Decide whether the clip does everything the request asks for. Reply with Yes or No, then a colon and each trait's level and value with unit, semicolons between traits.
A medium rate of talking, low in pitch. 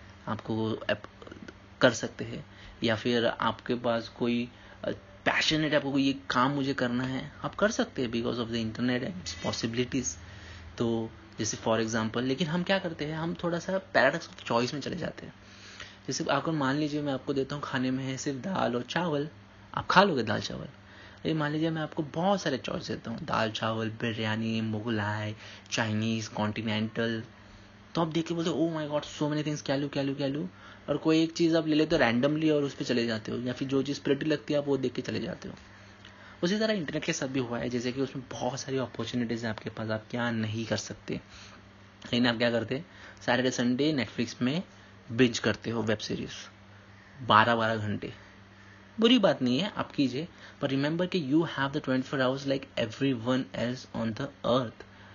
No: fast, 205 wpm; low, 125 Hz